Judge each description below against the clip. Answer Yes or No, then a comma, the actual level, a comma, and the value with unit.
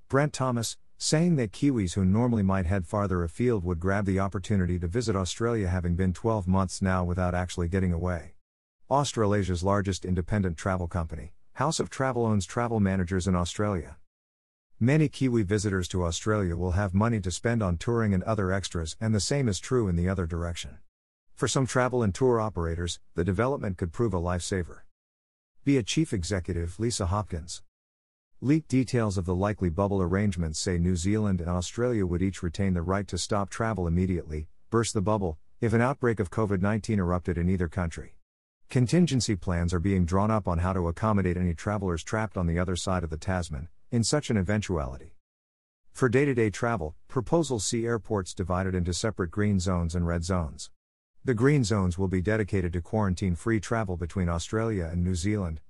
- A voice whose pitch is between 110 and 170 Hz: No, very low, 95 Hz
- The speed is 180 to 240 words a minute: Yes, average, 185 wpm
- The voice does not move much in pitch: No, average, 3.9 semitones